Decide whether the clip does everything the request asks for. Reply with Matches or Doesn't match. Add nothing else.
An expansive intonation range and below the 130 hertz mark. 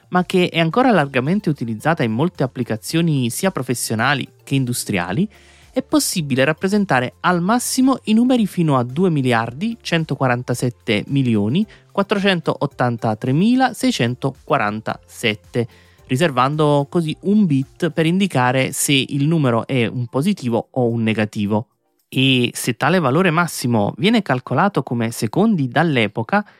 Doesn't match